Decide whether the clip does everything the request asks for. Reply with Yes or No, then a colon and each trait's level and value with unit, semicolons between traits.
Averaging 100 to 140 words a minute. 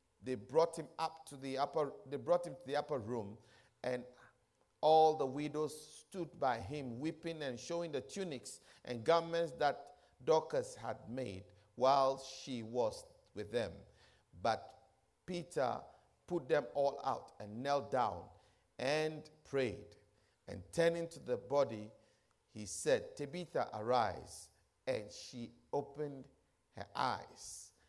Yes: slow, 135 wpm